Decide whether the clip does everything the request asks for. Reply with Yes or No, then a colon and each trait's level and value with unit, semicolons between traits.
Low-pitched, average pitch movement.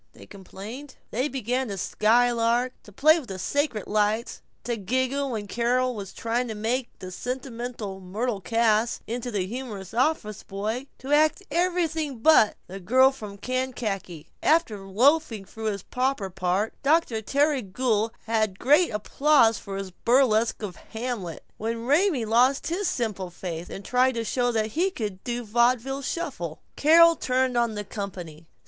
No: high, 235 Hz; average, 4.1 semitones